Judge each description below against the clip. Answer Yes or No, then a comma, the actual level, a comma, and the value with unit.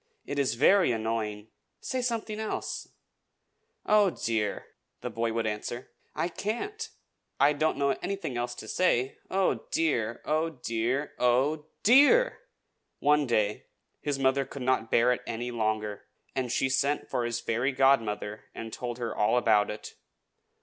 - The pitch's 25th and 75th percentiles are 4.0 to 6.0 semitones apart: Yes, average, 5.2 semitones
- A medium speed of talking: Yes, average, 150 wpm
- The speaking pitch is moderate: No, low, 130 Hz